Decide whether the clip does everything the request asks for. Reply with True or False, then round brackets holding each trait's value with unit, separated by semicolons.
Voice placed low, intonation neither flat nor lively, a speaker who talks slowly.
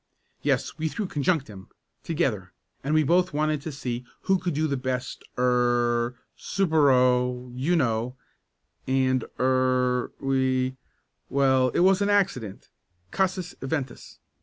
True (130 Hz; 4.0 semitones; 125 wpm)